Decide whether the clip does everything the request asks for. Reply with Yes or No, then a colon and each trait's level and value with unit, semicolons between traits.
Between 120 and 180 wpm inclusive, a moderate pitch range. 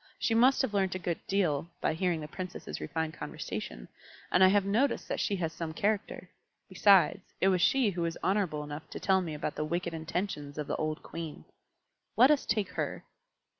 No: average, 200 wpm; average, 4.0 semitones